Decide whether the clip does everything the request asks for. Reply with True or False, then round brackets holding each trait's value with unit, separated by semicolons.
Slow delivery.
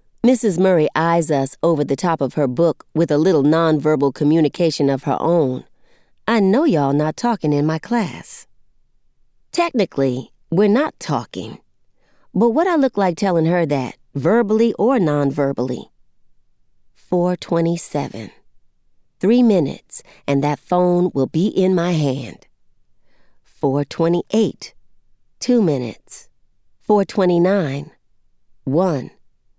True (115 wpm)